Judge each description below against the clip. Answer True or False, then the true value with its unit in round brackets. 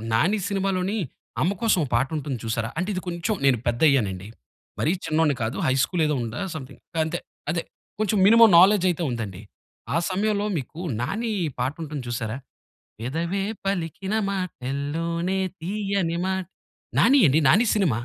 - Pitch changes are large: True (6.6 semitones)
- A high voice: False (165 Hz)